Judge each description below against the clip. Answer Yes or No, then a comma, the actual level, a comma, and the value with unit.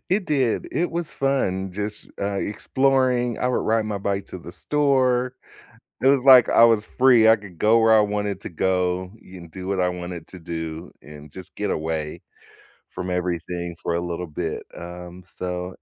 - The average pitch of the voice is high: No, very low, 95 Hz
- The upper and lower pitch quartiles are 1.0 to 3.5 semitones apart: No, wide, 5.4 semitones